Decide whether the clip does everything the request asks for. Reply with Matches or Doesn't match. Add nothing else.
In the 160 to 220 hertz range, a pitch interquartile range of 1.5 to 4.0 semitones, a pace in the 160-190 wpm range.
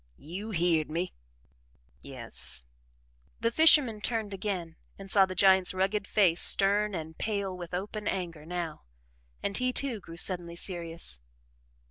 Doesn't match